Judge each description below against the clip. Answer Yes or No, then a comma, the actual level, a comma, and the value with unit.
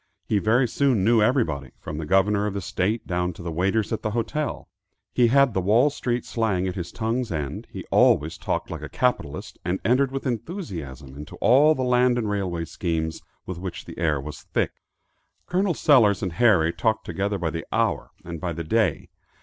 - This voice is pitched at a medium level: No, low, 100 Hz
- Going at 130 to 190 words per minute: No, average, 200 wpm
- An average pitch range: No, wide, 6.3 semitones